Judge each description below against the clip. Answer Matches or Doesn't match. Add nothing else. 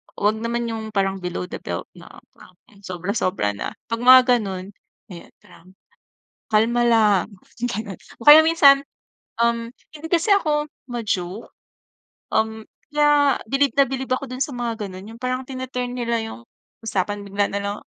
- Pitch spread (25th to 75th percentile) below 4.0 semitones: Doesn't match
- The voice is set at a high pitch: Matches